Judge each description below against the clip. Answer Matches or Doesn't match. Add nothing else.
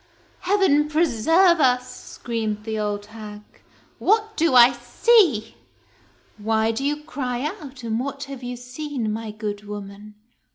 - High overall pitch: Matches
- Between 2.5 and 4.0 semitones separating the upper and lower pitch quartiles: Doesn't match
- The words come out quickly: Doesn't match